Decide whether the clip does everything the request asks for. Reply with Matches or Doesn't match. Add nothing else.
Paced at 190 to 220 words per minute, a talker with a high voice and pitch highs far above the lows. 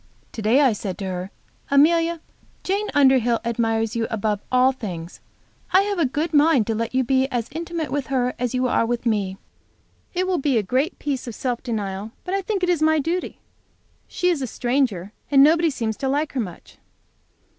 Matches